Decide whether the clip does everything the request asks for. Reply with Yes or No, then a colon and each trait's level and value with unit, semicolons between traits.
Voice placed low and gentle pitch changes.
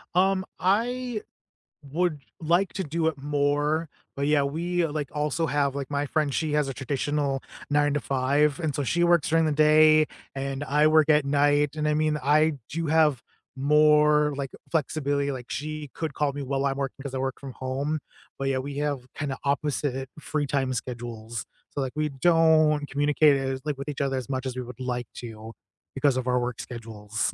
No: medium, 145 Hz; narrow, 2.3 semitones